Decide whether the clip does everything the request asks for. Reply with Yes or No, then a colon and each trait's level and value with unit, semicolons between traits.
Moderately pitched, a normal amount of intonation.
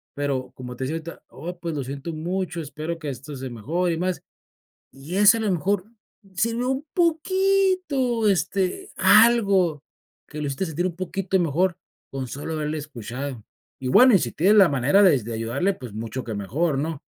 No: medium, 165 Hz; wide, 6.2 semitones